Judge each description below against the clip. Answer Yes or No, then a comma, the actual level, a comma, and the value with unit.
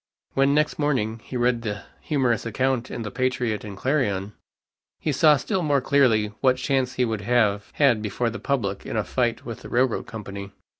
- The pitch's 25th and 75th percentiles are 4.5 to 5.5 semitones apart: No, average, 3.8 semitones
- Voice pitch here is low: Yes, low, 120 Hz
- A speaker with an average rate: Yes, average, 190 wpm